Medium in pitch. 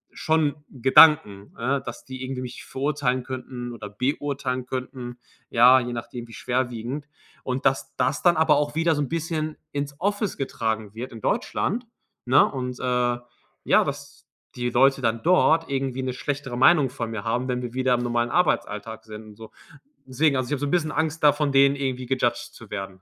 No: low, 130 Hz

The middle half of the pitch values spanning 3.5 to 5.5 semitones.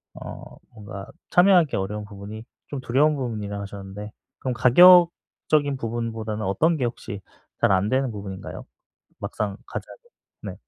Yes: average, 5.1 semitones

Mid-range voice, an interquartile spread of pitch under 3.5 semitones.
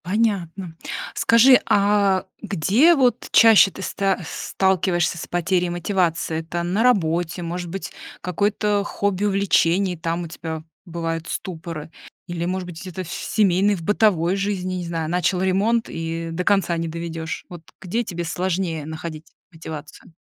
Yes: medium, 180 Hz; average, 3.1 semitones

